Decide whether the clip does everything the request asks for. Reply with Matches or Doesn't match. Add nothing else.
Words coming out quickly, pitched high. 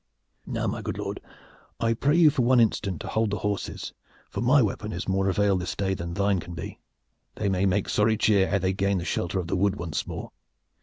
Doesn't match